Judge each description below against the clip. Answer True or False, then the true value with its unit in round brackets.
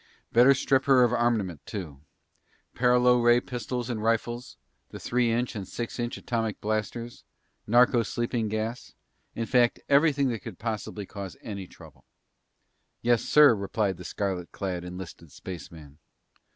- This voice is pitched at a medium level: False (115 Hz)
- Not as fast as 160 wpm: True (140 wpm)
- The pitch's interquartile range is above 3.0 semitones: True (3.6 semitones)